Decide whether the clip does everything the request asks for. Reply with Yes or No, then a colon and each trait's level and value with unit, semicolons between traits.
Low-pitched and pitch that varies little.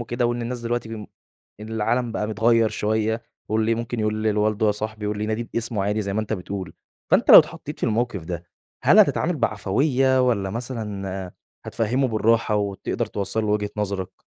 Yes: low, 110 Hz; narrow, 2.0 semitones